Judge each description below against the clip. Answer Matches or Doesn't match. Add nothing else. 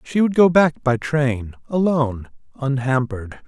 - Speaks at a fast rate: Doesn't match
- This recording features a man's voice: Matches